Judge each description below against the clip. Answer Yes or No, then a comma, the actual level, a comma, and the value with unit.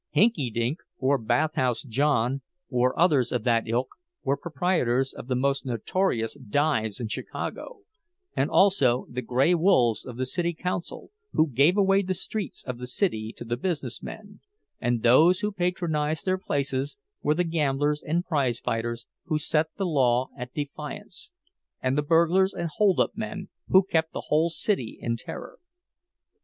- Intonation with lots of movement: Yes, wide, 6.2 semitones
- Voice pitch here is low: No, medium, 145 Hz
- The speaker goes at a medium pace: Yes, average, 160 wpm